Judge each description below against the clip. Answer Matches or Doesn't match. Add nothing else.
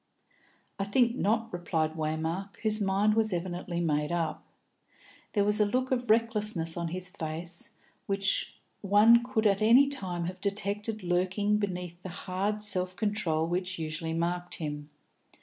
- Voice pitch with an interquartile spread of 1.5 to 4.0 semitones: Matches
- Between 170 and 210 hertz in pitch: Matches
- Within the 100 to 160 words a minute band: Matches